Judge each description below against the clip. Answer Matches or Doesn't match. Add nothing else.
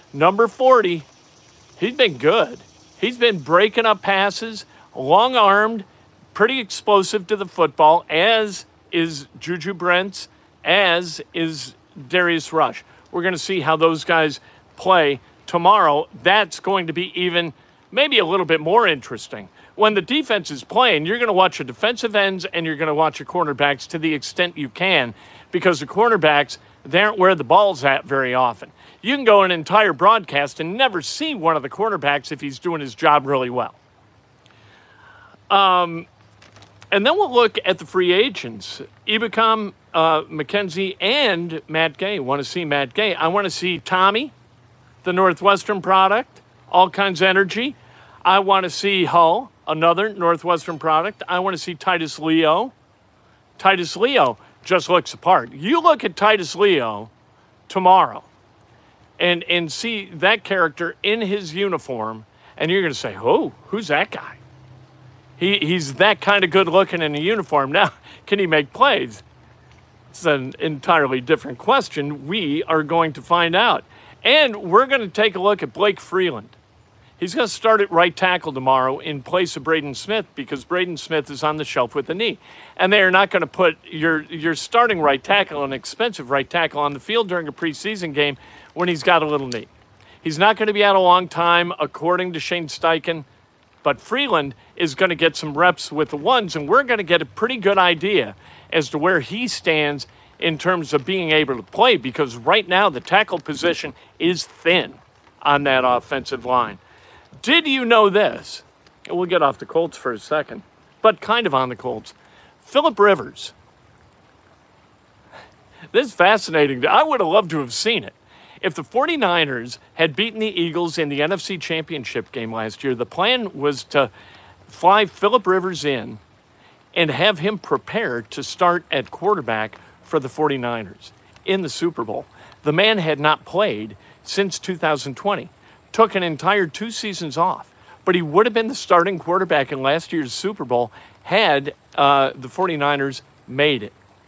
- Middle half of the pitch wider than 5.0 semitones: Matches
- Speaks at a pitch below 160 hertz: Doesn't match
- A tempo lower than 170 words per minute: Doesn't match